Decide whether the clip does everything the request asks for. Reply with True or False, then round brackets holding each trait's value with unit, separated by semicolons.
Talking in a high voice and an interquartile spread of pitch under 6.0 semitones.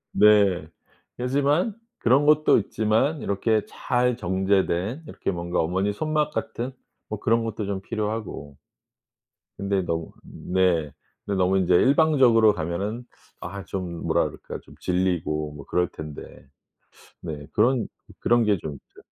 False (100 Hz; 5.1 semitones)